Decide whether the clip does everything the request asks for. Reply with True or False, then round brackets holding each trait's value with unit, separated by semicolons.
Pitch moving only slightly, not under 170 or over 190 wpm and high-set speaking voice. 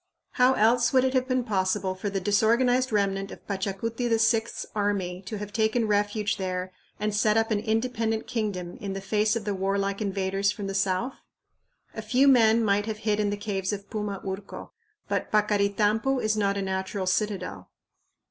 True (2.3 semitones; 180 wpm; 210 Hz)